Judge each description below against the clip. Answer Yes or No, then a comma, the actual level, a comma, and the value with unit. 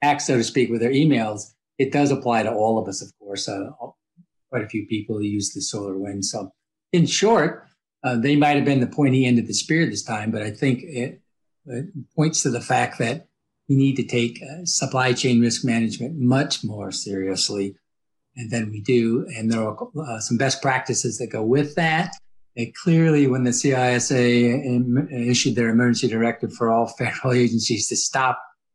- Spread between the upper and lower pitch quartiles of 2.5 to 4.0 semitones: Yes, average, 3.6 semitones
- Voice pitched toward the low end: Yes, low, 120 Hz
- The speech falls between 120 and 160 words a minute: No, average, 190 wpm